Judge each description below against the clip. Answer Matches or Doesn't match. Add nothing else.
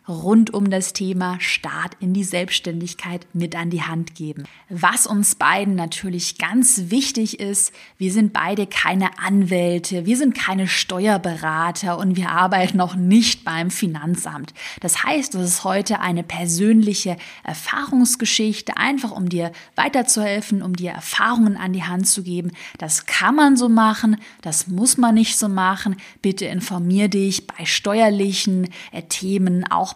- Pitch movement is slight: Doesn't match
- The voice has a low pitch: Doesn't match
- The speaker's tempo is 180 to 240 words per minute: Doesn't match